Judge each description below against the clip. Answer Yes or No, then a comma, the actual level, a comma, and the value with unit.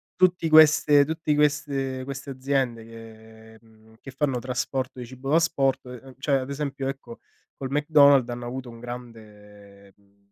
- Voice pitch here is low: Yes, low, 130 Hz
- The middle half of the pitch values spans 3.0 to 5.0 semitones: Yes, average, 3.5 semitones